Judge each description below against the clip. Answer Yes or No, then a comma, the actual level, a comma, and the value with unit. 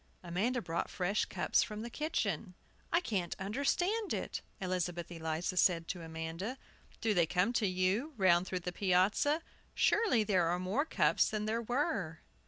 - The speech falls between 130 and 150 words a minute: No, average, 165 wpm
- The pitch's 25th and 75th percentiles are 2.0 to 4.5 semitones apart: No, average, 5.0 semitones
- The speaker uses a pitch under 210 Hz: Yes, high, 190 Hz